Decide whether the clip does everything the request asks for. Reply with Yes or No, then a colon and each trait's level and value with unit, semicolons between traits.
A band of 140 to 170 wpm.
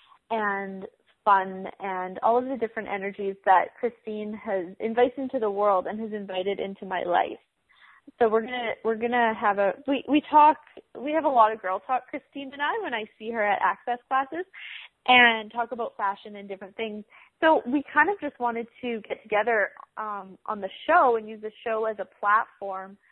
No: average, 195 wpm